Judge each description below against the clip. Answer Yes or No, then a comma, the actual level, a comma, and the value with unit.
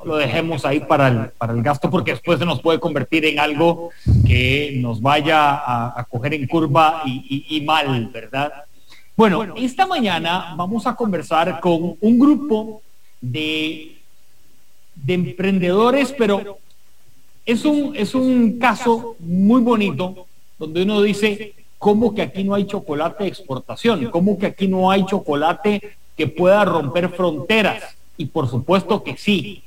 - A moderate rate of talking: Yes, average, 150 wpm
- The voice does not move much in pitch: No, wide, 5.5 semitones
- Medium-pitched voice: Yes, medium, 175 Hz